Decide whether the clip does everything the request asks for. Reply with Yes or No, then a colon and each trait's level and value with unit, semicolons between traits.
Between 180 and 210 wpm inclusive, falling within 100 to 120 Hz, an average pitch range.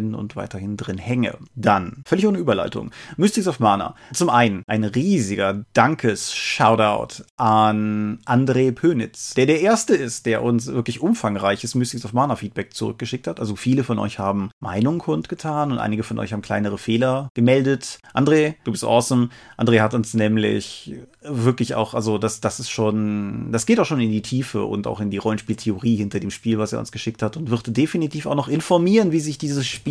Yes: fast, 190 wpm; low, 115 Hz; average, 3.6 semitones